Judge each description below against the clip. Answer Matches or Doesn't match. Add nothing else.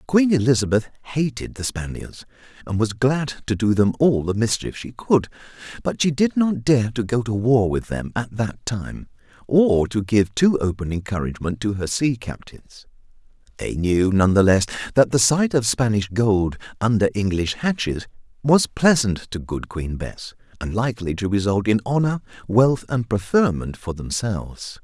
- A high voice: Doesn't match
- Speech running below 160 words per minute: Doesn't match